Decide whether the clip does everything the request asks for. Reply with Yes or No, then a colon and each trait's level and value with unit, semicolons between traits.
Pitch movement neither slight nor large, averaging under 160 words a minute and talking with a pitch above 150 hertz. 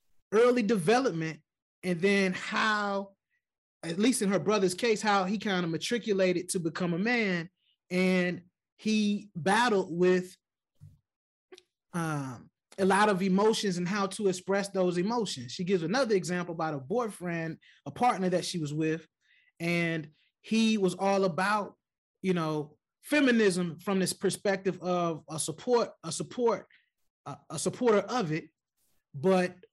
Yes: average, 3.6 semitones; average, 140 wpm; high, 190 Hz